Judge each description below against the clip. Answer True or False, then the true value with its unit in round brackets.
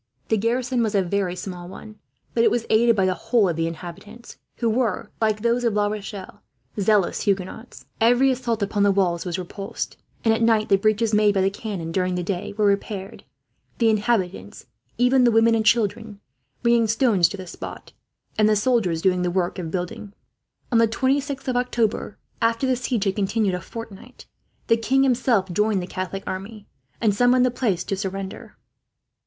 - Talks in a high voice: True (210 Hz)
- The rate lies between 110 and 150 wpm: False (190 wpm)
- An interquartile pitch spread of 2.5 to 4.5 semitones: True (3.4 semitones)